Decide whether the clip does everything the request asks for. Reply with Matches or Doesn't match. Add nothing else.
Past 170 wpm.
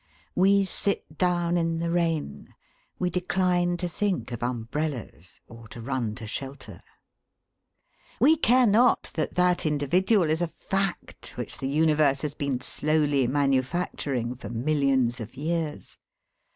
Doesn't match